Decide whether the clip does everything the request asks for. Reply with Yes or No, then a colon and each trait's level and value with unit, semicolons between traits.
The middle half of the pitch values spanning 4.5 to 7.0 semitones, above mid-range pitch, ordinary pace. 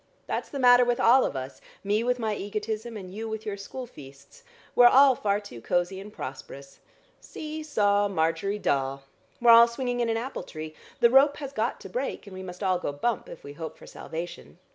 No: wide, 5.5 semitones; high, 210 Hz; fast, 210 wpm